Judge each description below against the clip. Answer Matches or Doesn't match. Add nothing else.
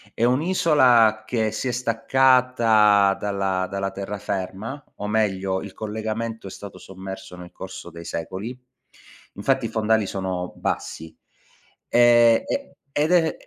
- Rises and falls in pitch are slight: Doesn't match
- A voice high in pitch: Doesn't match